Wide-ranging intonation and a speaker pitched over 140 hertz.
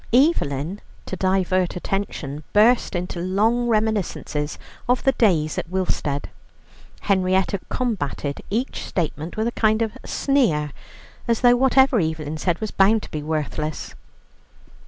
Yes: wide, 6.2 semitones; high, 190 Hz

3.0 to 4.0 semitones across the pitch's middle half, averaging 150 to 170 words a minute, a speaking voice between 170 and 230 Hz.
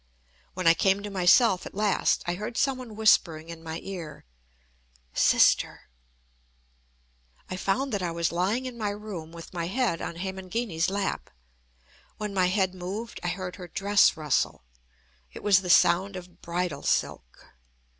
Yes: average, 3.3 semitones; average, 155 wpm; medium, 185 Hz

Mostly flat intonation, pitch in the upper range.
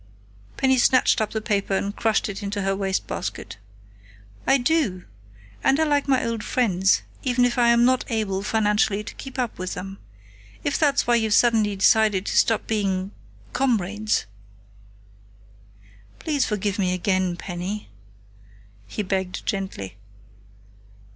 No: average, 4.0 semitones; high, 210 Hz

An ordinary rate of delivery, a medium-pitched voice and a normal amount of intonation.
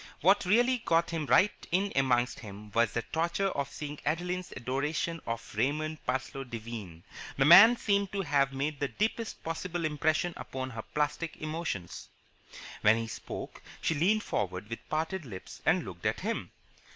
No: average, 160 wpm; medium, 150 Hz; wide, 6.1 semitones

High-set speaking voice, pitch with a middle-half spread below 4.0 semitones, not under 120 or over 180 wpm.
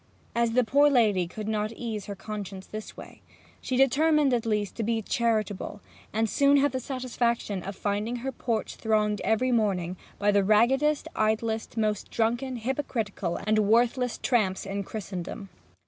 Yes: high, 220 Hz; average, 3.0 semitones; average, 160 wpm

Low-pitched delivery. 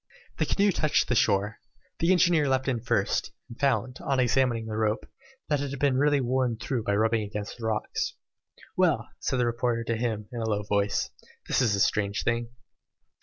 Yes: low, 120 Hz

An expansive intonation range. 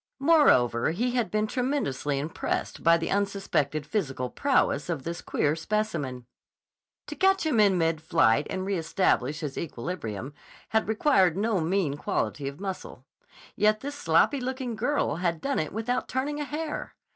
Yes: wide, 8.3 semitones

